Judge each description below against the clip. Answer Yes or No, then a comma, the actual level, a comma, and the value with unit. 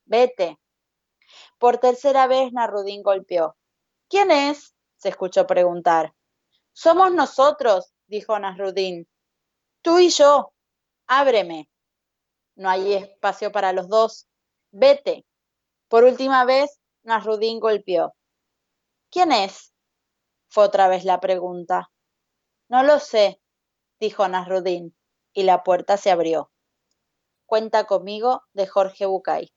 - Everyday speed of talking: No, slow, 110 wpm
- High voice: Yes, high, 205 Hz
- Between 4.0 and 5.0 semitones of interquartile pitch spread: No, wide, 5.4 semitones